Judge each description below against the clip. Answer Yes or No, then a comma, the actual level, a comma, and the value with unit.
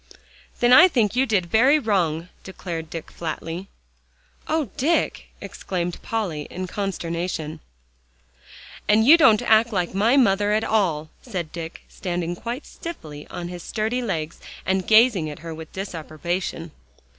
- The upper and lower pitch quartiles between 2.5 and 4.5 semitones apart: No, average, 5.0 semitones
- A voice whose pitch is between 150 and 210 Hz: Yes, high, 190 Hz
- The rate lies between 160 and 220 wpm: No, average, 140 wpm